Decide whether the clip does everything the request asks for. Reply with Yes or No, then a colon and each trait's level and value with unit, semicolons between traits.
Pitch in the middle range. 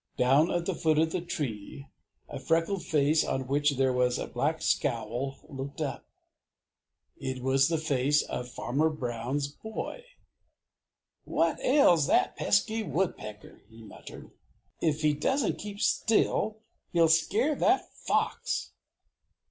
Yes: medium, 150 Hz